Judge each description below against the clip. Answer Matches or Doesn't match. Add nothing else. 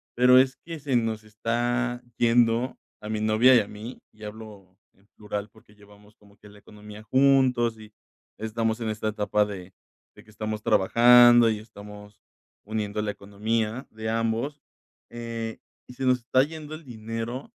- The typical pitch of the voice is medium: Doesn't match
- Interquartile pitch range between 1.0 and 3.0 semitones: Matches